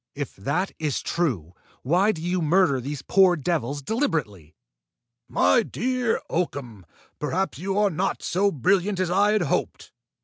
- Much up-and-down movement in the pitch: Yes, wide, 5.7 semitones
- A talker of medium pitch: Yes, medium, 170 Hz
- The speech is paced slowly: No, average, 145 wpm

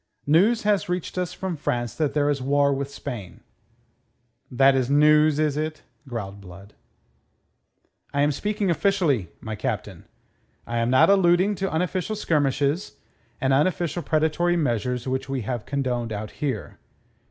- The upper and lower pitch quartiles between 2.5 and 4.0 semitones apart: No, wide, 5.5 semitones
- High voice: No, medium, 145 Hz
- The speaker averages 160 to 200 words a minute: No, average, 145 wpm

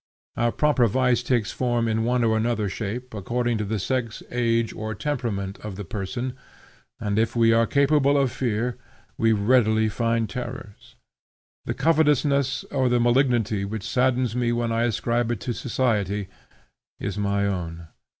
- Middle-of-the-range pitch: No, low, 115 Hz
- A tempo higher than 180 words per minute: No, average, 160 wpm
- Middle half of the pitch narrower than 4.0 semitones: Yes, average, 2.7 semitones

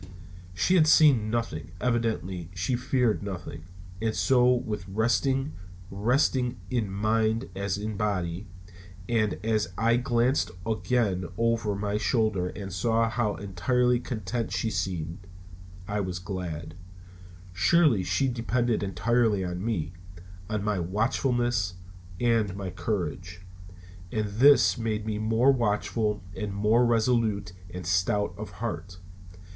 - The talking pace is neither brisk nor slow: No, slow, 125 wpm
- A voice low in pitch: Yes, low, 110 Hz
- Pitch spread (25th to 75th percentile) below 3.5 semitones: No, average, 3.9 semitones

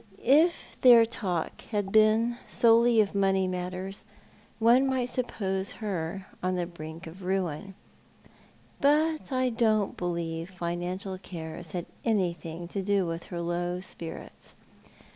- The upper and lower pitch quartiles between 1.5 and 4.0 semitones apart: No, average, 4.5 semitones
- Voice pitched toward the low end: No, high, 190 Hz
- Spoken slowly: Yes, slow, 125 wpm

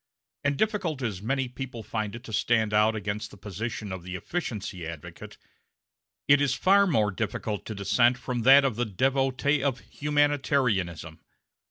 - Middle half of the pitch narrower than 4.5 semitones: No, average, 4.9 semitones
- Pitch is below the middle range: Yes, low, 120 Hz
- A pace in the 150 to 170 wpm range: Yes, average, 160 wpm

